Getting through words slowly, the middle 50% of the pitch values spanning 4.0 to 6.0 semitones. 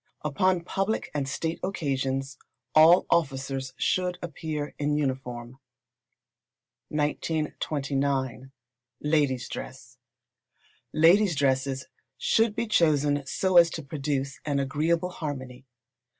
No: slow, 95 wpm; average, 3.6 semitones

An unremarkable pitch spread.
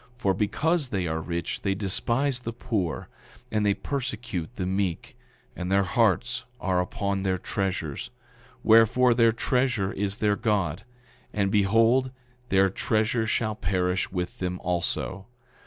Yes: average, 3.6 semitones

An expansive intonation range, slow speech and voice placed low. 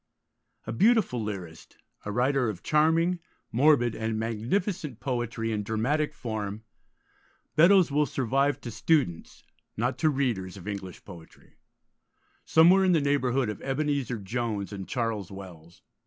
Yes: wide, 5.9 semitones; slow, 130 wpm; low, 120 Hz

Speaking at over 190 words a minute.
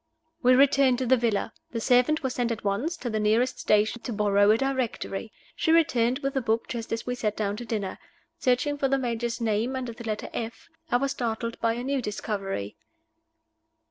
Yes: fast, 205 wpm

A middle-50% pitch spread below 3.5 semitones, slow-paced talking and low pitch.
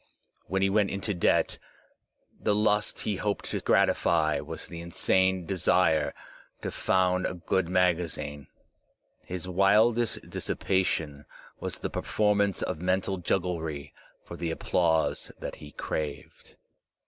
Yes: average, 3.1 semitones; slow, 125 wpm; very low, 90 Hz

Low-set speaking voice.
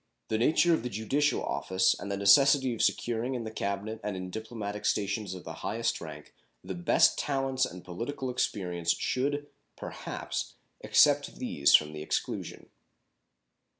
Yes: low, 110 Hz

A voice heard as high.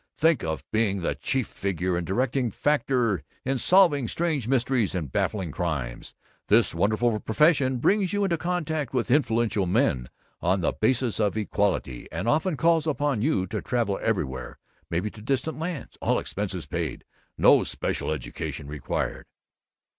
No: low, 115 Hz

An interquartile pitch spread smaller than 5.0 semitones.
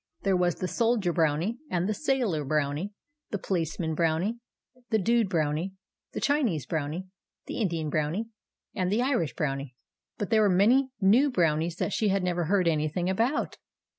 No: average, 5.3 semitones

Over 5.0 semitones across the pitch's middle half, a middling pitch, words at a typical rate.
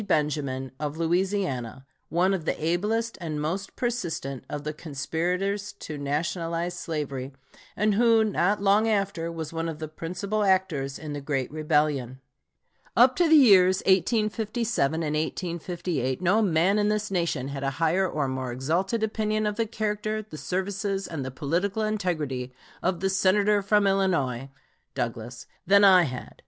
Yes: wide, 5.4 semitones; medium, 175 Hz; average, 155 wpm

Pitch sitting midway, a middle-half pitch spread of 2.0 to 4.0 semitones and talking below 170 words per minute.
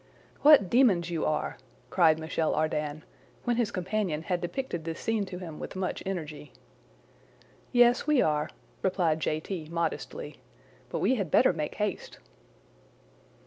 No: medium, 175 Hz; average, 4.8 semitones; average, 145 wpm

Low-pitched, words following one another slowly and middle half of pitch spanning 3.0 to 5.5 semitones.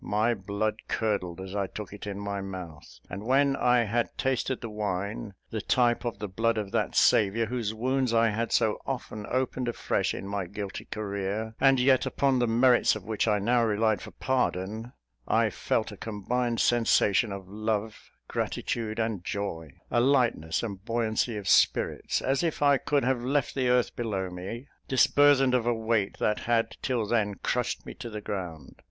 No: low, 110 Hz; average, 185 wpm; average, 3.3 semitones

